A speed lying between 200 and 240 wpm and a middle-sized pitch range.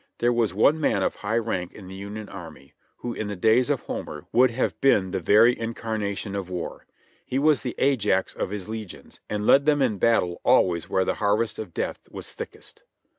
Yes: fast, 205 wpm; average, 3.8 semitones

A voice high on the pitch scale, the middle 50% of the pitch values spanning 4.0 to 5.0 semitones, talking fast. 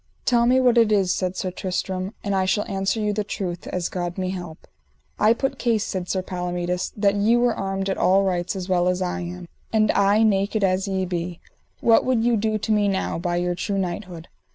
No: high, 195 Hz; average, 2.9 semitones; fast, 225 wpm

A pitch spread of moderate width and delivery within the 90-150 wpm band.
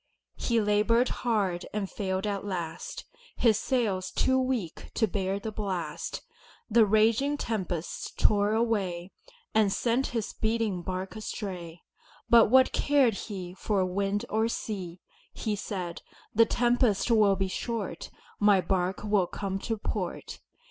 Yes: average, 3.3 semitones; slow, 135 wpm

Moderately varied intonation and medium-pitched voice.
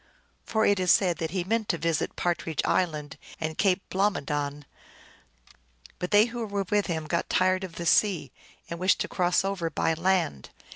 Yes: average, 3.3 semitones; medium, 180 Hz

